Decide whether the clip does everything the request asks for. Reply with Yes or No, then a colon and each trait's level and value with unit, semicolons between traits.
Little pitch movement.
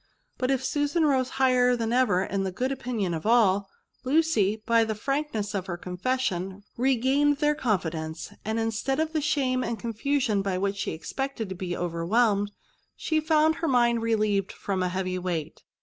No: wide, 5.6 semitones